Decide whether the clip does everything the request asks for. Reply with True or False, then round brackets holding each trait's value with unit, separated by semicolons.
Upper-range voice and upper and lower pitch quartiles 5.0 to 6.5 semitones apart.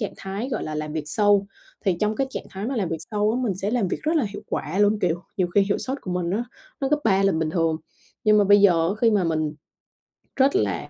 False (200 Hz; 3.9 semitones)